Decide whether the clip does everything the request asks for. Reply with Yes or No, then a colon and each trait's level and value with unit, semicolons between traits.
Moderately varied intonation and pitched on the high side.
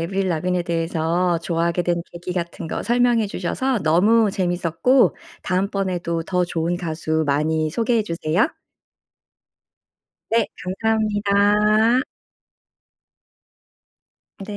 No: average, 4.0 semitones; medium, 180 Hz